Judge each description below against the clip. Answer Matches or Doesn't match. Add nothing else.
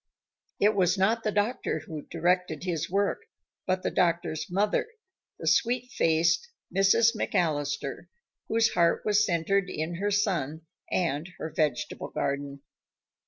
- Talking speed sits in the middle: Doesn't match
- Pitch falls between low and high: Matches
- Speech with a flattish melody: Doesn't match